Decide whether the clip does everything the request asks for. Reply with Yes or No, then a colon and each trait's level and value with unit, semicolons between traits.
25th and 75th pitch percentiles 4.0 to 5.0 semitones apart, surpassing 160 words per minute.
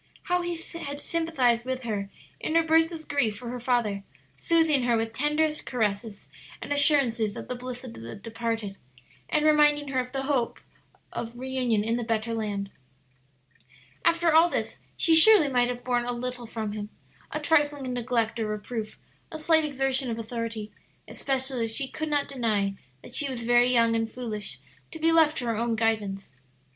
Yes: average, 4.5 semitones; average, 185 wpm